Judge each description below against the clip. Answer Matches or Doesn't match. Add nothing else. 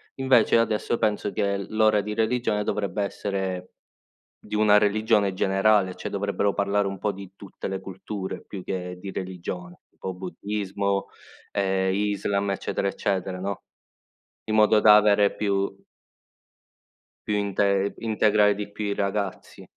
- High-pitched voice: Doesn't match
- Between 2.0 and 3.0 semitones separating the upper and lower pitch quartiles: Doesn't match